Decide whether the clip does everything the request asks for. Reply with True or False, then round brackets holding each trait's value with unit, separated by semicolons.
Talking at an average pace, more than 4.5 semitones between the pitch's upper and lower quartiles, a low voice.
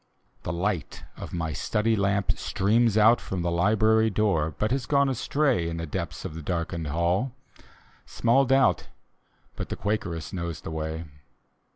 True (160 wpm; 5.0 semitones; 95 Hz)